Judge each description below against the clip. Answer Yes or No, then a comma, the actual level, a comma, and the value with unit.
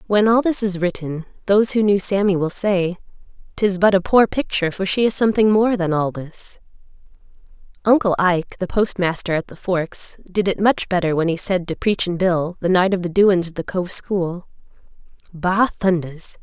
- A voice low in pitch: No, high, 190 Hz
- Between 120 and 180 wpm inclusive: No, average, 190 wpm